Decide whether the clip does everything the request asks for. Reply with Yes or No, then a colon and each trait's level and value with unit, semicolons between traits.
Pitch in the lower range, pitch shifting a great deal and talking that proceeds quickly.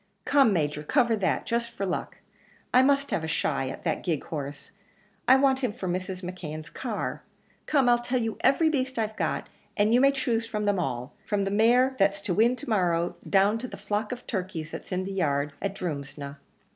No: high, 205 Hz; wide, 6.1 semitones; fast, 210 wpm